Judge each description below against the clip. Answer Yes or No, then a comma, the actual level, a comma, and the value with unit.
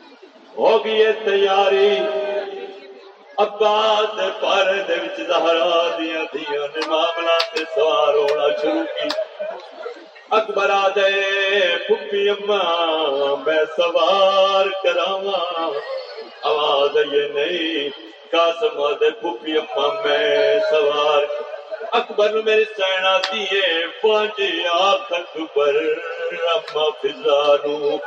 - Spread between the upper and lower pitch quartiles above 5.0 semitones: Yes, wide, 5.4 semitones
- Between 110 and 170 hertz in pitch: No, high, 195 Hz